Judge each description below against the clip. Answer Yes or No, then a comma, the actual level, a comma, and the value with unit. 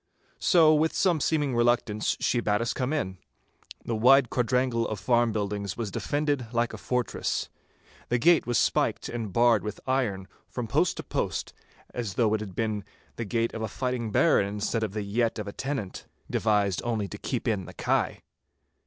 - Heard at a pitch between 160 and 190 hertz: No, low, 115 Hz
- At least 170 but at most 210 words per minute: Yes, average, 190 wpm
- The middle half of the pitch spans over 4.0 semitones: No, average, 3.2 semitones